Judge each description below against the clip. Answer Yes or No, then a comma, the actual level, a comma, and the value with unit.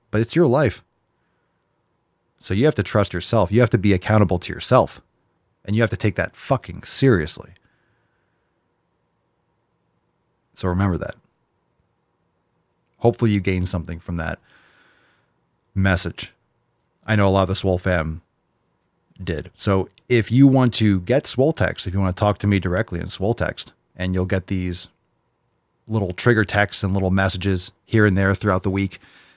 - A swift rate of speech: No, average, 160 wpm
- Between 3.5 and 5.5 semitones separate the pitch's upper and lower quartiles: No, average, 3.1 semitones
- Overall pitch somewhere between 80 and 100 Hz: Yes, very low, 95 Hz